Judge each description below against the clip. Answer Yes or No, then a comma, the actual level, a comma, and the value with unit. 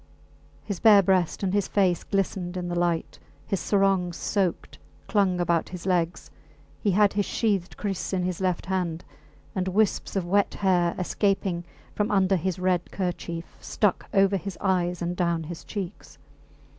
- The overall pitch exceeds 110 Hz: Yes, medium, 185 Hz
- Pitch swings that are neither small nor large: No, narrow, 2.1 semitones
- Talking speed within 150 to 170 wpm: Yes, average, 160 wpm